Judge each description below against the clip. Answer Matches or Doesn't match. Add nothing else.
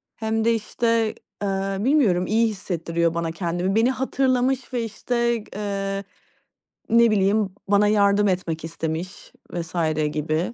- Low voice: Doesn't match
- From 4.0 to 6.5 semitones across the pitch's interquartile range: Matches